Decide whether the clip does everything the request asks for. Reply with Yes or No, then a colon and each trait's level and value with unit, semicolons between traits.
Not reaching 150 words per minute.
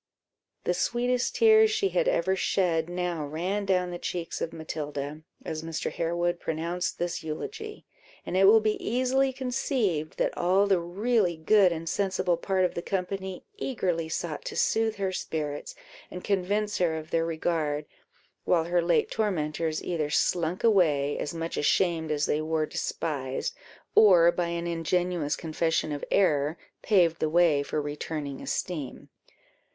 No: average, 155 wpm